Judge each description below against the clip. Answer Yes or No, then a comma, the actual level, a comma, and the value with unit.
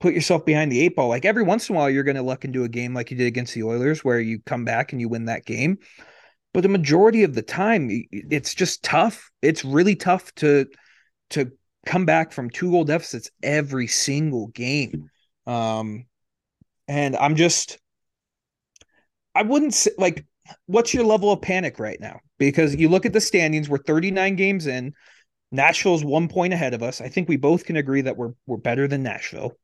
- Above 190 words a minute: Yes, average, 200 wpm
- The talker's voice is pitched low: No, medium, 145 Hz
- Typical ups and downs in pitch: No, wide, 6.4 semitones